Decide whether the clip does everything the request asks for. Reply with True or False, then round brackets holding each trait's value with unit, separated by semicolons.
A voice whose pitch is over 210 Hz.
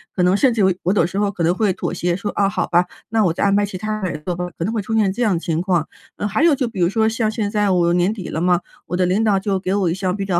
False (195 Hz)